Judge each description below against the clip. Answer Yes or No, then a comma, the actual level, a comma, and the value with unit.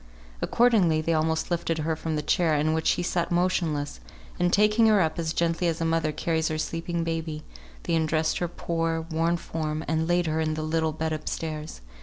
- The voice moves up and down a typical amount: No, narrow, 1.5 semitones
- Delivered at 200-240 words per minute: Yes, fast, 205 wpm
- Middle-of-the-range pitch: Yes, medium, 160 Hz